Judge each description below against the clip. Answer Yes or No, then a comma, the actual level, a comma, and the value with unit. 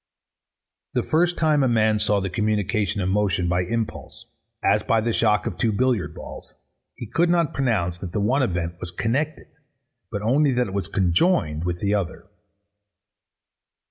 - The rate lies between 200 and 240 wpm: No, average, 170 wpm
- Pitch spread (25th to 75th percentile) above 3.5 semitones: Yes, average, 5.1 semitones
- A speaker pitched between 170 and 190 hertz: No, low, 105 Hz